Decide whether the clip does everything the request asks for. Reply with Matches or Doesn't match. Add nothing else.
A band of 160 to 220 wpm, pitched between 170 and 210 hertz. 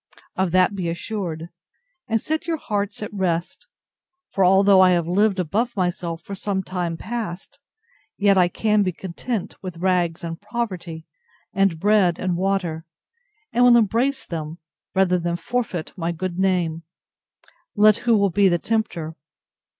Doesn't match